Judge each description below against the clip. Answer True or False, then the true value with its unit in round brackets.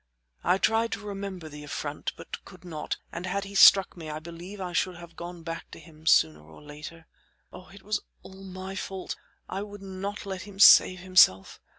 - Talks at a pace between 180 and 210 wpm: True (200 wpm)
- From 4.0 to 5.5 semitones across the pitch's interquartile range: False (2.9 semitones)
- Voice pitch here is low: False (185 Hz)